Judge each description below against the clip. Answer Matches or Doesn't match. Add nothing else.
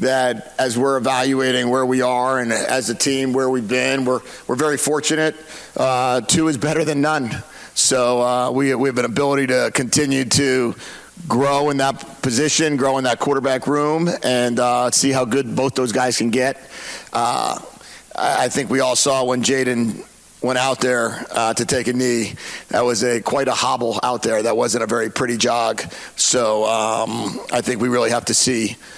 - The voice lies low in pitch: Matches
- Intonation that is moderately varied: Doesn't match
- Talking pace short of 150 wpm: Doesn't match